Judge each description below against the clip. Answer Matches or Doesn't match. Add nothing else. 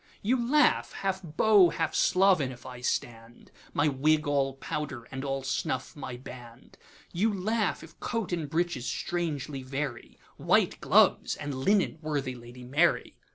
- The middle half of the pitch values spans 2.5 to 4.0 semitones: Doesn't match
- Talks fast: Doesn't match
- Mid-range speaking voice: Matches